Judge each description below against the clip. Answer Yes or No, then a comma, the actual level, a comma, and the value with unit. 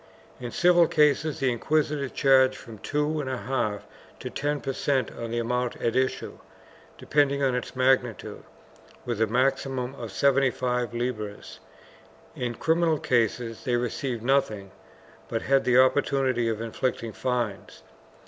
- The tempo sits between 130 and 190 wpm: Yes, average, 145 wpm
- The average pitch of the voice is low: Yes, low, 130 Hz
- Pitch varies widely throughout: No, average, 2.7 semitones